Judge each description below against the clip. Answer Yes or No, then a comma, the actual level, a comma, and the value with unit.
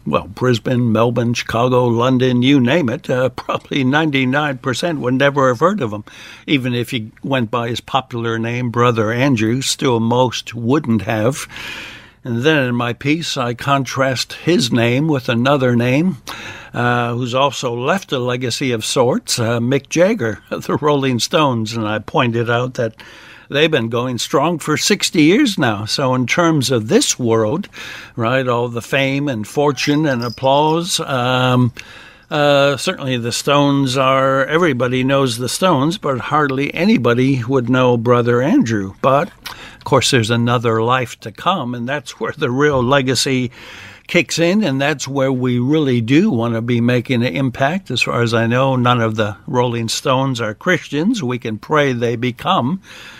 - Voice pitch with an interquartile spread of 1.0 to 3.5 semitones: Yes, average, 2.9 semitones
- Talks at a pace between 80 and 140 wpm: No, average, 165 wpm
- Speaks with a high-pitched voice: No, low, 125 Hz